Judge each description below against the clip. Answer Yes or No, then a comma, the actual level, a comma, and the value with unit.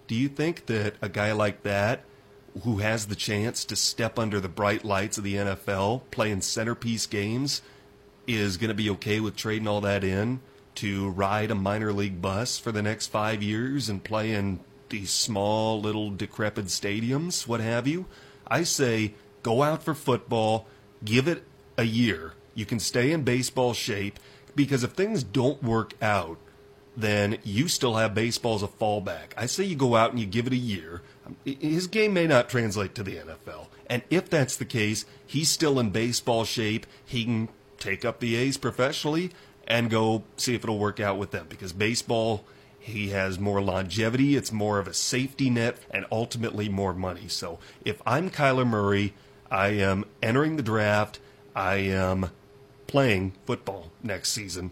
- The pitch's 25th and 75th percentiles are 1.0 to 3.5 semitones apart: No, average, 3.9 semitones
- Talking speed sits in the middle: Yes, average, 180 wpm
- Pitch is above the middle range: No, low, 110 Hz